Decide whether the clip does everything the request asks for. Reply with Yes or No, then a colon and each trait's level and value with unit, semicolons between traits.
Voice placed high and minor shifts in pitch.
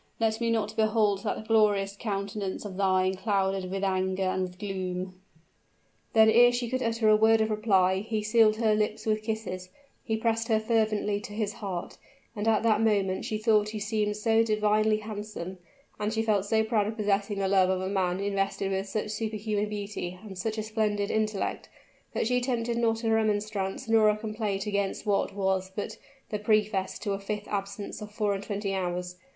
Yes: high, 210 Hz; narrow, 1.9 semitones